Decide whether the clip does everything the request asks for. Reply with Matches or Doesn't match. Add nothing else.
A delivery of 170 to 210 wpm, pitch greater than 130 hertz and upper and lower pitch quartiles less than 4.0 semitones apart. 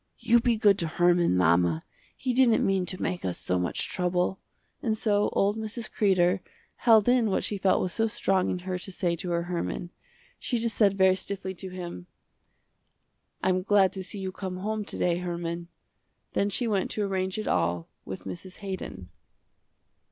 Matches